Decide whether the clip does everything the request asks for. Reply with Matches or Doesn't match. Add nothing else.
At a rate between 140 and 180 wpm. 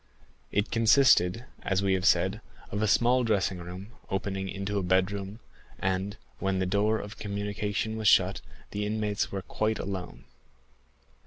Matches